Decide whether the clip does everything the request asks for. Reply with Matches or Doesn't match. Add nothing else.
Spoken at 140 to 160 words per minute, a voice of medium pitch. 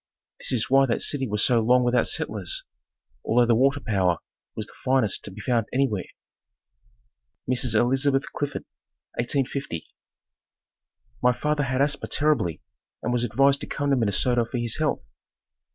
Doesn't match